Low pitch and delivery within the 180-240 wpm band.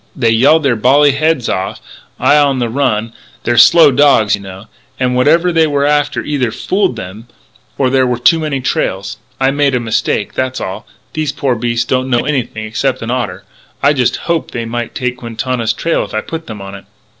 Yes: low, 130 Hz; average, 200 wpm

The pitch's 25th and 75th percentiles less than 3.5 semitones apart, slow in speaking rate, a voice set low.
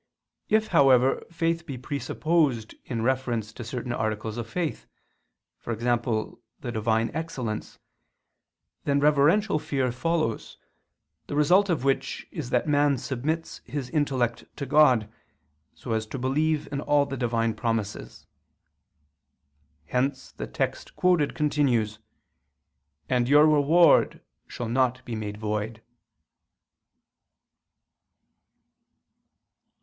No: average, 4.3 semitones; slow, 110 wpm; low, 130 Hz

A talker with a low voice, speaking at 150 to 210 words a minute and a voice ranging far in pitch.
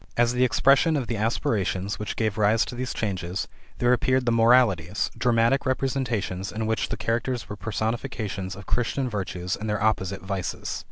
No: low, 110 Hz; average, 170 wpm; average, 3.7 semitones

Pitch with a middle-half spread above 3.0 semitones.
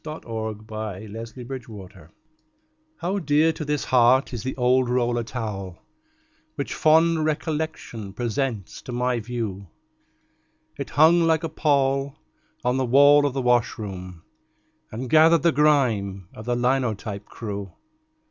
Yes: average, 5.1 semitones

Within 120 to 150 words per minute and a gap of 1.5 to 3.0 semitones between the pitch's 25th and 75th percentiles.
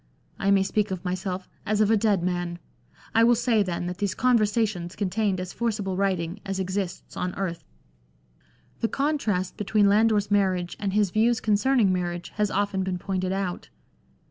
No: average, 170 wpm; narrow, 2.6 semitones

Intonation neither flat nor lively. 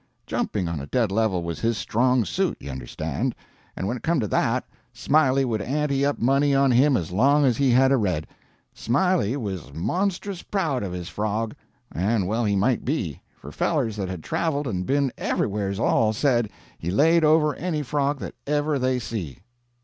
No: wide, 6.3 semitones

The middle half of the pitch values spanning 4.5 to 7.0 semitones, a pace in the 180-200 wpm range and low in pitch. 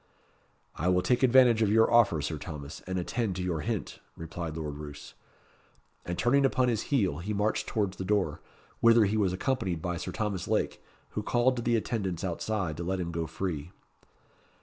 Yes: average, 5.0 semitones; average, 190 wpm; very low, 95 Hz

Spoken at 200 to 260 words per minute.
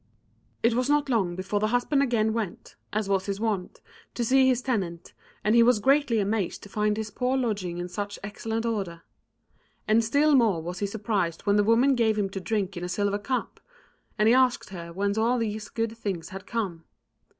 Yes: fast, 205 wpm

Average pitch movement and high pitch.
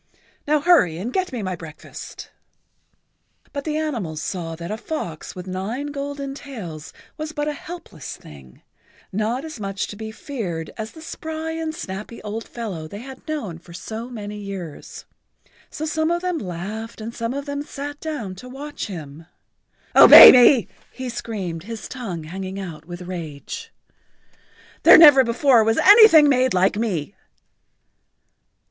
No: wide, 7.8 semitones; high, 225 Hz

